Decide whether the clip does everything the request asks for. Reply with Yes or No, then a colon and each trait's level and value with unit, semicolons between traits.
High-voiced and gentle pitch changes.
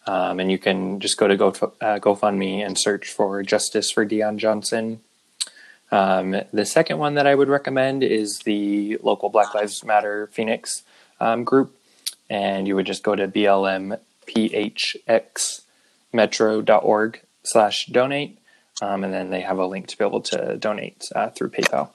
No: low, 105 Hz; narrow, 2.3 semitones